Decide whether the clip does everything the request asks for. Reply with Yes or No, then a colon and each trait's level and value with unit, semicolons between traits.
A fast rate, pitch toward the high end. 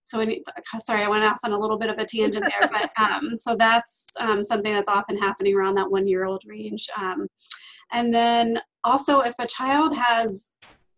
No: average, 185 wpm; high, 220 Hz